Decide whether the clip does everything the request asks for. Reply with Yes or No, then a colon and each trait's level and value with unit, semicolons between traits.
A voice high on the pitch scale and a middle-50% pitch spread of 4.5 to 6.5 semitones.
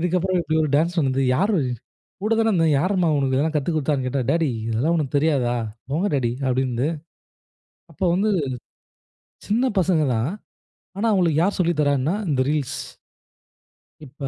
No: medium, 155 Hz; average, 4.9 semitones